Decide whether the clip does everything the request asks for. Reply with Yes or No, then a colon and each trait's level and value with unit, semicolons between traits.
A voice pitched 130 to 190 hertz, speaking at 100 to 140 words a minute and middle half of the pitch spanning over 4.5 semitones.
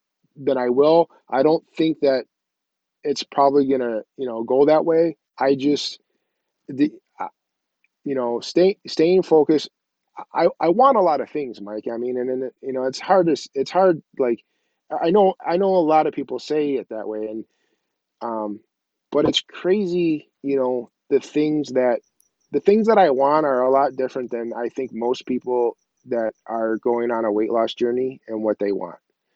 No: low, 135 Hz; average, 190 wpm; average, 5.0 semitones